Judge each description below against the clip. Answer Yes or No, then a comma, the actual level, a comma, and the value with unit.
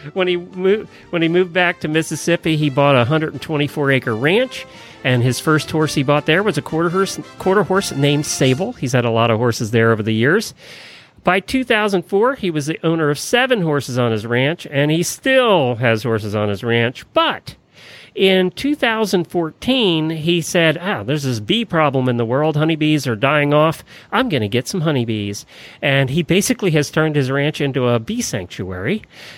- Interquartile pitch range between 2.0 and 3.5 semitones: No, wide, 5.6 semitones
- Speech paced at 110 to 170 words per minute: No, average, 195 wpm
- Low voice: No, medium, 155 Hz